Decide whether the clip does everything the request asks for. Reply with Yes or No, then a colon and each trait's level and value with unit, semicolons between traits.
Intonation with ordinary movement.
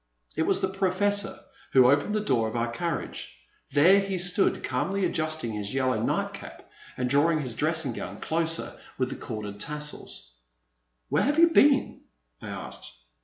No: wide, 7.9 semitones